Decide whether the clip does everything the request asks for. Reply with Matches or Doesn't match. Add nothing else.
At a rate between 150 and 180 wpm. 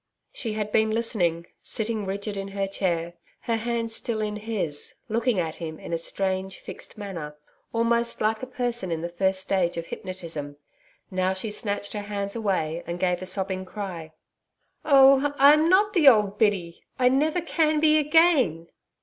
Matches